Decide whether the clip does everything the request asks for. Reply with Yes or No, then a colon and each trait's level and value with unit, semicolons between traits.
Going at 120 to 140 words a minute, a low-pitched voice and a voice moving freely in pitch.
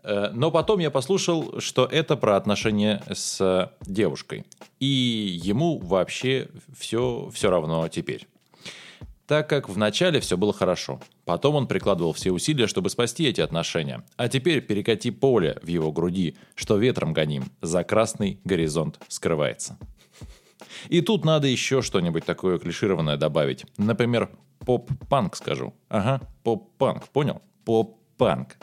Yes: average, 130 wpm; low, 110 Hz; wide, 6.8 semitones